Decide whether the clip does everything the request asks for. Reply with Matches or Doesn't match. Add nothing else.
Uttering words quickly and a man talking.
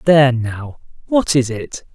Doesn't match